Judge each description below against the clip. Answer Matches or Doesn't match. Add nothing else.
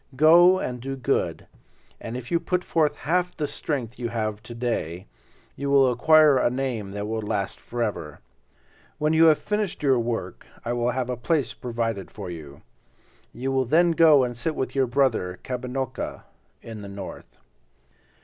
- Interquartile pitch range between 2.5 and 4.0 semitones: Doesn't match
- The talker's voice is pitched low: Matches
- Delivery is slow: Doesn't match